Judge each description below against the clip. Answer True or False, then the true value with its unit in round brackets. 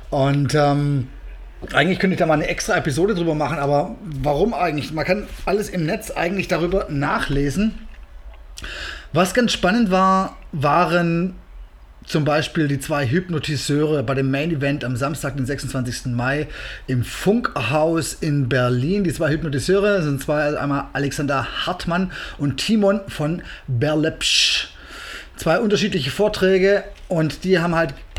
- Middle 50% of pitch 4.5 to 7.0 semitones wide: True (4.9 semitones)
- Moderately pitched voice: True (150 Hz)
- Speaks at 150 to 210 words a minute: False (140 wpm)